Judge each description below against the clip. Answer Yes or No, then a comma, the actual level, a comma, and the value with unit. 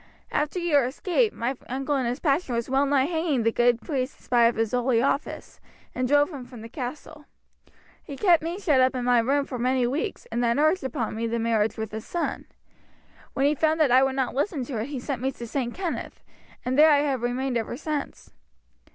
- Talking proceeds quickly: Yes, fast, 225 wpm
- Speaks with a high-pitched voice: Yes, very high, 265 Hz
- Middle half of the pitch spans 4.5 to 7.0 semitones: No, average, 3.5 semitones